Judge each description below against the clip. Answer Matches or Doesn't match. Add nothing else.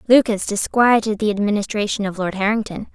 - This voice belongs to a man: Doesn't match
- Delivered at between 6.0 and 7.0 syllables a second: Doesn't match